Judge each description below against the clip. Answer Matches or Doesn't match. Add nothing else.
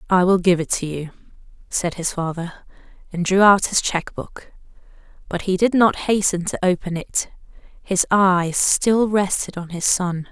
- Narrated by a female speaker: Matches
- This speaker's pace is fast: Doesn't match